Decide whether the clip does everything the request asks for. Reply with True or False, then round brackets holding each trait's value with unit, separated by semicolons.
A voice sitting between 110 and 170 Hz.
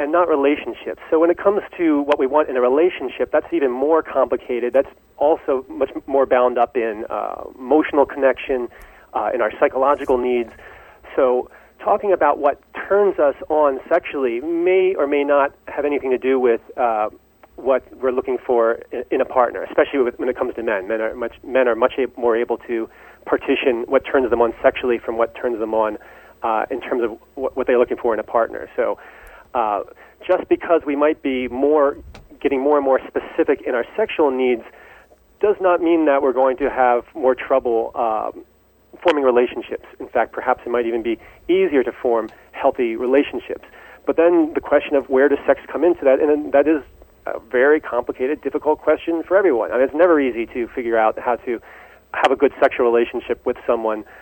True (140 Hz)